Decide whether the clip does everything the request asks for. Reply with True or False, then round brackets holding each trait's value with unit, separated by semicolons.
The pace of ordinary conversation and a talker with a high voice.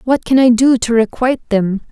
False (220 wpm; 240 Hz)